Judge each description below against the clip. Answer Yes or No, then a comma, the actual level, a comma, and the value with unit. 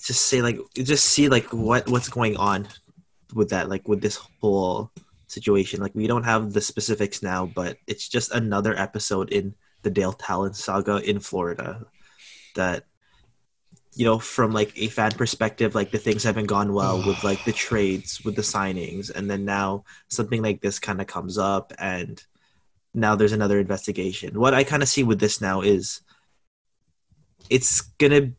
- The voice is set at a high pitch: No, low, 105 Hz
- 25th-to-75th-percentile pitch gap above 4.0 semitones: No, average, 2.8 semitones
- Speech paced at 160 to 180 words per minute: Yes, average, 175 wpm